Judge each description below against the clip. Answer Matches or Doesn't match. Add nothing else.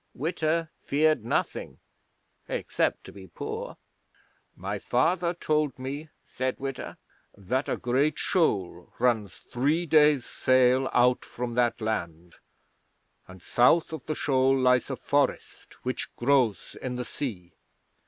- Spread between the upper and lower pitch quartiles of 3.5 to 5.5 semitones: Matches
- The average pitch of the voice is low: Matches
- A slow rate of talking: Matches